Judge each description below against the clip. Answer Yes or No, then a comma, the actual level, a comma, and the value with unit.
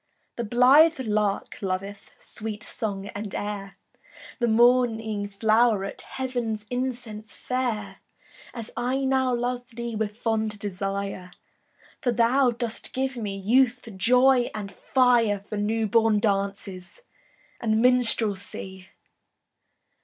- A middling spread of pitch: Yes, average, 3.3 semitones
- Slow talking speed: Yes, slow, 110 wpm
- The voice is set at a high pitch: Yes, high, 225 Hz